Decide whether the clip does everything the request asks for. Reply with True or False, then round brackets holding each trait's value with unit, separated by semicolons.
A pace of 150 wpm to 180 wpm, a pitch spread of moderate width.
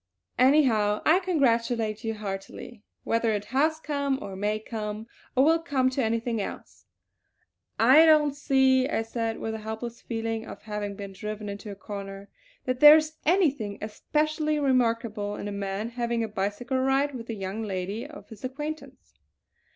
True (165 wpm; 4.6 semitones)